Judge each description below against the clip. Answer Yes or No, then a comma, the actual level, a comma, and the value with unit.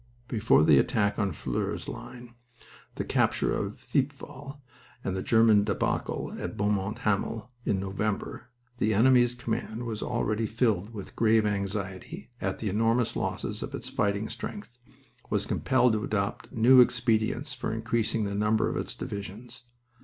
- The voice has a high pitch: No, low, 110 Hz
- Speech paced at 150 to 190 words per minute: Yes, average, 155 wpm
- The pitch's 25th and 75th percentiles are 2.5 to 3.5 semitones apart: Yes, average, 2.8 semitones